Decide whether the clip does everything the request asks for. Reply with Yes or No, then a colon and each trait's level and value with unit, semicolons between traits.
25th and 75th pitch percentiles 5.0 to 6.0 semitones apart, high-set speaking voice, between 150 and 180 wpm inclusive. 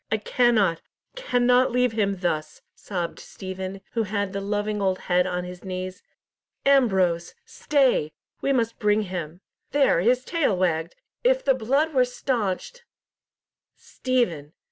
No: wide, 5.5 semitones; high, 205 Hz; slow, 135 wpm